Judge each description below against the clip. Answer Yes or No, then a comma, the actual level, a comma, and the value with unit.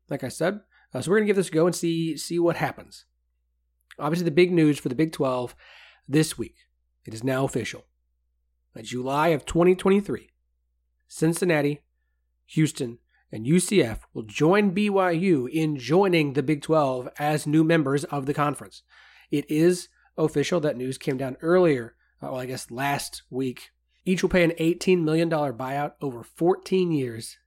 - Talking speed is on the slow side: No, average, 165 wpm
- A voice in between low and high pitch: Yes, medium, 145 Hz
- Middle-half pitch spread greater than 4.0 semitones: Yes, average, 5.2 semitones